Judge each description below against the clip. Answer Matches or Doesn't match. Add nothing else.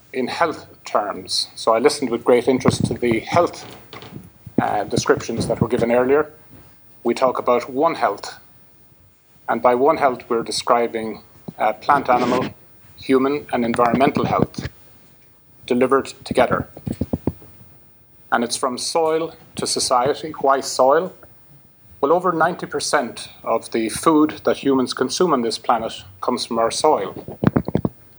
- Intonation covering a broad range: Doesn't match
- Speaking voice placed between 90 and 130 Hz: Matches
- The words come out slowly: Matches